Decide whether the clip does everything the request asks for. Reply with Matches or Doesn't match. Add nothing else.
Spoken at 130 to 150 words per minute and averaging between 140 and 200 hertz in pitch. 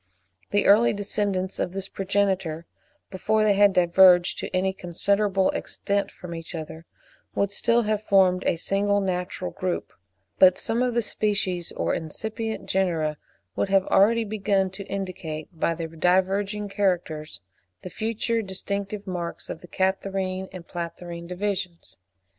Matches